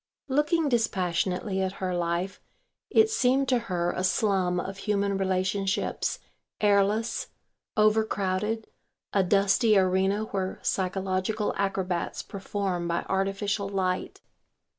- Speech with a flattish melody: Yes, narrow, 2.2 semitones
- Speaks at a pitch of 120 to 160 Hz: No, high, 195 Hz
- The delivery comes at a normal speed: No, slow, 110 wpm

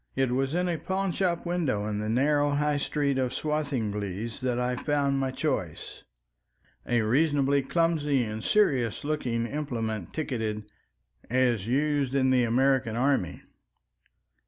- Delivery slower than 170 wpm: Yes, slow, 135 wpm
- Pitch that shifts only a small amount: No, average, 4.2 semitones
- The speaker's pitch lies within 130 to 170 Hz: Yes, low, 135 Hz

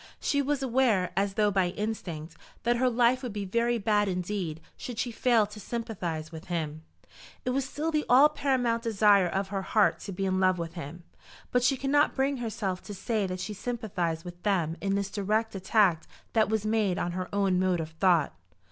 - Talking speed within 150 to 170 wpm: No, fast, 205 wpm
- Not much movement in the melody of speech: No, average, 4.4 semitones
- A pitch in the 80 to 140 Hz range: No, high, 205 Hz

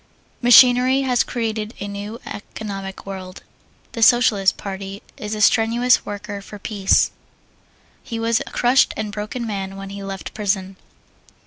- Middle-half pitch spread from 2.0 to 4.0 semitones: Yes, average, 2.8 semitones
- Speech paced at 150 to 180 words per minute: No, average, 140 wpm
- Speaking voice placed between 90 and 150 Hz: No, high, 210 Hz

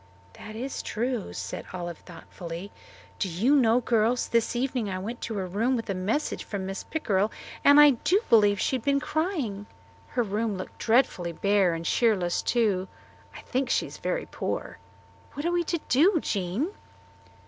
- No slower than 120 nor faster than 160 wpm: No, average, 175 wpm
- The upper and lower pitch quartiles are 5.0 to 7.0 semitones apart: Yes, average, 5.3 semitones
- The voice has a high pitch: Yes, high, 225 Hz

